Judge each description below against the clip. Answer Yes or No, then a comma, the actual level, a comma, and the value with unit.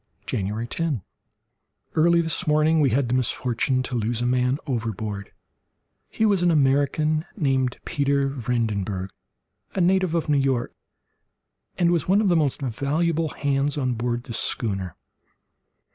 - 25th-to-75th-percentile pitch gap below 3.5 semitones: No, average, 4.8 semitones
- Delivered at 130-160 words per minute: Yes, average, 140 wpm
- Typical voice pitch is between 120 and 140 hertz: Yes, low, 135 Hz